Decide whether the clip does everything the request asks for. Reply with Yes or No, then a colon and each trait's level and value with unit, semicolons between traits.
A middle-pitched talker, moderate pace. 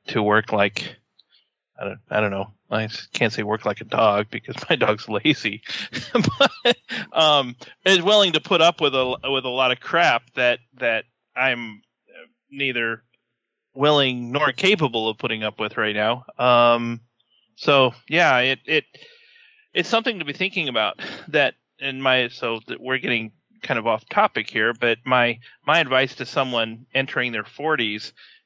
No: low, 125 Hz; average, 165 wpm